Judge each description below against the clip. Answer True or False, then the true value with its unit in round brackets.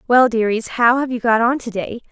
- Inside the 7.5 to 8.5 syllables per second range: False (5.4 syllables/s)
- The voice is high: True (235 Hz)